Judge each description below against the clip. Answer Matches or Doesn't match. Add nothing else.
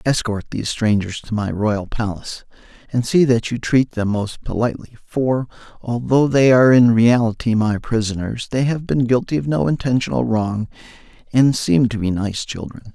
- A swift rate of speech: Doesn't match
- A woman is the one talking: Doesn't match